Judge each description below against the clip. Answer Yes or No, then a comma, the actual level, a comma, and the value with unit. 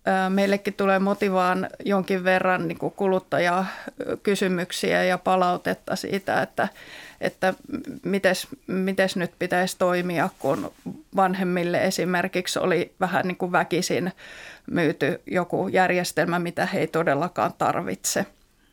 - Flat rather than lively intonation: Yes, narrow, 1.4 semitones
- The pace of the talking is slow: No, average, 105 wpm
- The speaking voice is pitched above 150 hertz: Yes, medium, 185 Hz